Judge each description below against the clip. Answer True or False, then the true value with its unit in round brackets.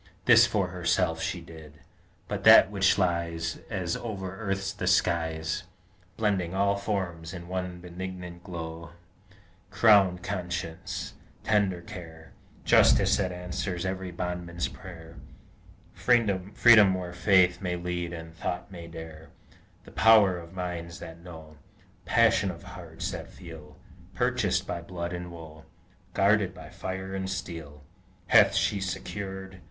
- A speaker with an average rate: False (130 wpm)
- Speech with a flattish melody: True (2.2 semitones)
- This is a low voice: True (90 Hz)